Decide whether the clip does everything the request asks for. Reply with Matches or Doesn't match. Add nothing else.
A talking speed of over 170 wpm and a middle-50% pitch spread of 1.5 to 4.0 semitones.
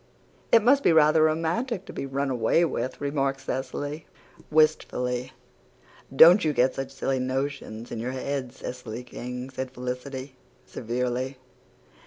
Doesn't match